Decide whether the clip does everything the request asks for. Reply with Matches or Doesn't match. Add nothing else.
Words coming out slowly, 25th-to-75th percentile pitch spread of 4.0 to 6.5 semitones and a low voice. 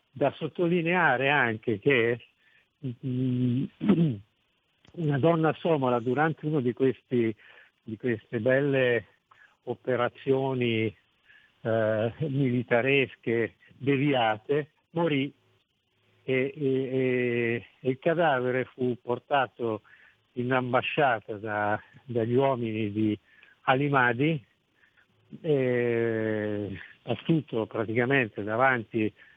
Doesn't match